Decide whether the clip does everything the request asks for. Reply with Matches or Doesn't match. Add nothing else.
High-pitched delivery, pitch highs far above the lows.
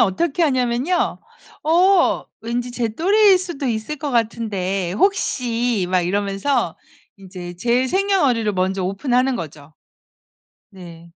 Matches